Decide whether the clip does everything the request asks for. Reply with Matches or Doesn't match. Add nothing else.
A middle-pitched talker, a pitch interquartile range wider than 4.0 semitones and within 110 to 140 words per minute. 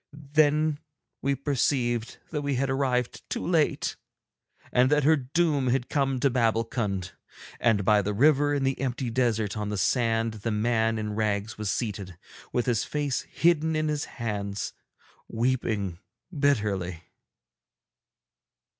Doesn't match